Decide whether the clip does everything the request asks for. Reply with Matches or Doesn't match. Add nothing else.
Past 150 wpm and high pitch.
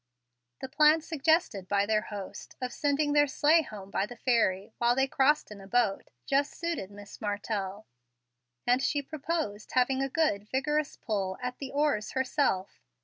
Matches